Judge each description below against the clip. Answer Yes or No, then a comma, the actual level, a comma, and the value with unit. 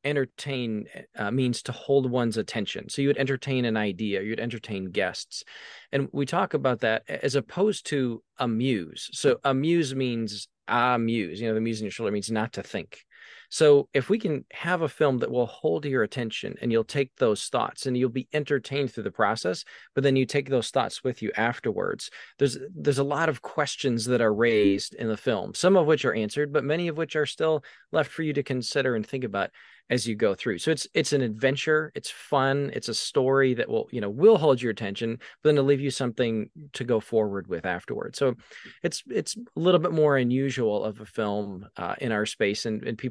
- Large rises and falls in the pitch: No, average, 4.3 semitones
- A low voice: Yes, low, 130 Hz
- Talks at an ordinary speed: No, fast, 215 wpm